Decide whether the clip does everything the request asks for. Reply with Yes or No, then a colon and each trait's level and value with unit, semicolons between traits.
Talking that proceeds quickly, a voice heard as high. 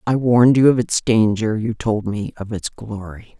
No: fast, 210 wpm; low, 115 Hz